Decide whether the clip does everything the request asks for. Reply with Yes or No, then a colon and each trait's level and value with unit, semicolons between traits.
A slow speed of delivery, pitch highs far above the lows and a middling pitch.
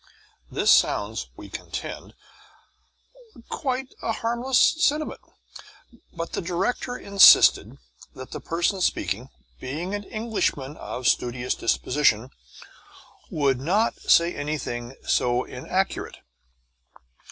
Yes: slow, 95 wpm; wide, 8.9 semitones; medium, 170 Hz